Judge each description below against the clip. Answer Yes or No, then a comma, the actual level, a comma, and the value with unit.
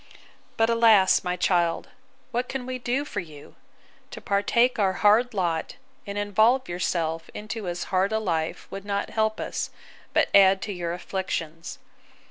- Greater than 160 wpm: No, average, 150 wpm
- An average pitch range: Yes, average, 4.0 semitones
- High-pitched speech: Yes, high, 200 Hz